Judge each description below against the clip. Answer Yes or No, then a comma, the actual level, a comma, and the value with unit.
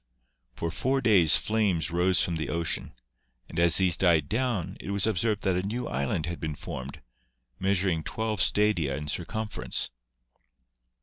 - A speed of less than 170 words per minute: Yes, average, 150 wpm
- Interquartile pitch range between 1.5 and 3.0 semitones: No, average, 4.4 semitones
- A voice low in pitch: Yes, very low, 90 Hz